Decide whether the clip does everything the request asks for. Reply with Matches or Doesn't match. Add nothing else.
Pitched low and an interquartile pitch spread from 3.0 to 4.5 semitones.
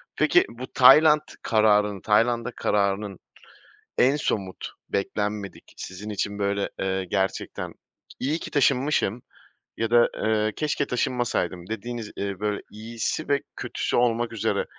Matches